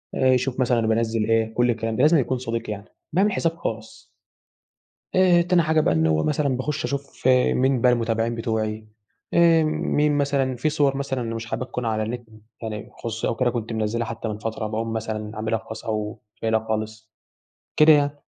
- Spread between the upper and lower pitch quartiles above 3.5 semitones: Yes, average, 3.9 semitones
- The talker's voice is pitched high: No, low, 115 Hz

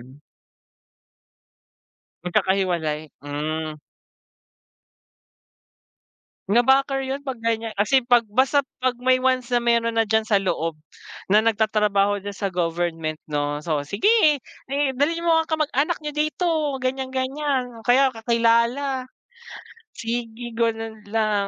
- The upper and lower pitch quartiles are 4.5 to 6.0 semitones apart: Yes, average, 5.0 semitones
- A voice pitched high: Yes, high, 230 Hz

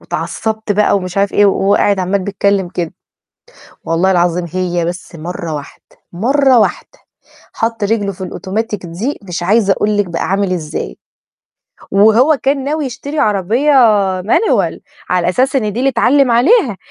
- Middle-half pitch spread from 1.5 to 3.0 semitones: No, average, 4.6 semitones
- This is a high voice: Yes, high, 200 Hz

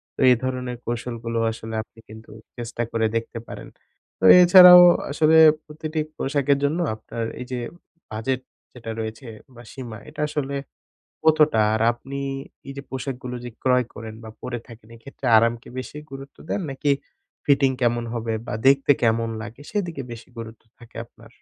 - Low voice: Yes, low, 125 Hz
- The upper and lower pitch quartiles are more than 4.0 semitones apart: No, average, 3.3 semitones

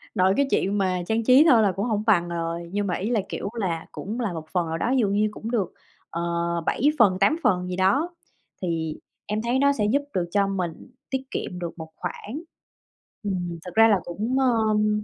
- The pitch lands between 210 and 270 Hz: No, high, 200 Hz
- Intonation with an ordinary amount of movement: Yes, average, 4.0 semitones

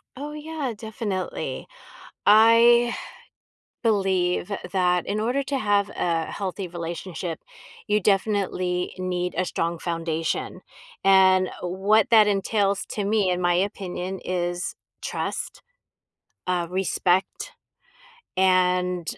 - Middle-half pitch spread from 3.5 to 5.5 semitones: No, average, 2.8 semitones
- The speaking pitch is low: No, high, 190 Hz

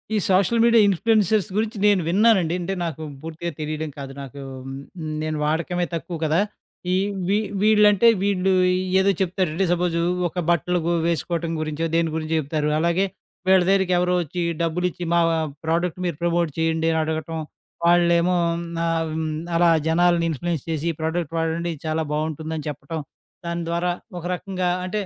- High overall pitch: No, medium, 170 Hz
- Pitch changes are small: Yes, narrow, 2.2 semitones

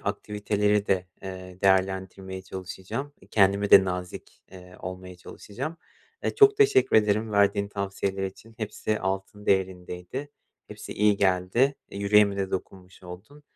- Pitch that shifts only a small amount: Yes, narrow, 2.0 semitones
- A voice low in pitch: Yes, low, 100 Hz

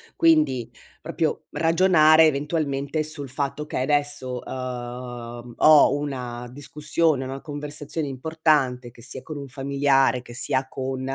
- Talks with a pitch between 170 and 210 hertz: No, medium, 140 Hz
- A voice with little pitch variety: No, average, 3.1 semitones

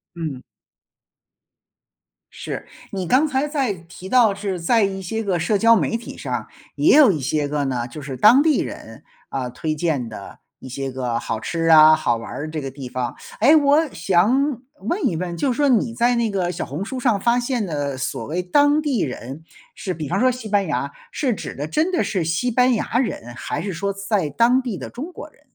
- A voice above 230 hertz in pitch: No, high, 190 Hz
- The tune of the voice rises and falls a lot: Yes, wide, 8.4 semitones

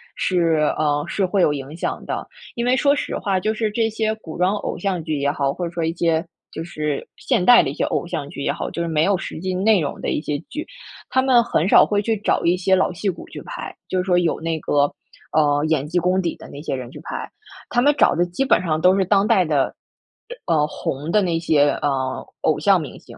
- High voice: No, medium, 175 Hz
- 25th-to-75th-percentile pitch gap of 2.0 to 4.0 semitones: No, average, 4.6 semitones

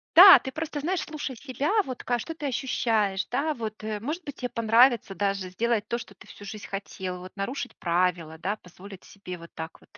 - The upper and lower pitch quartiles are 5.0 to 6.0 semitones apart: Yes, wide, 5.5 semitones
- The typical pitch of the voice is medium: No, high, 220 Hz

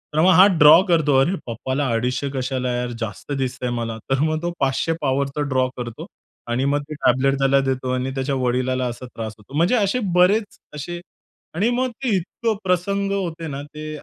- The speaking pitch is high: No, medium, 140 Hz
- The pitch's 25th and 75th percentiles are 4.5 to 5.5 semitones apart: Yes, average, 5.2 semitones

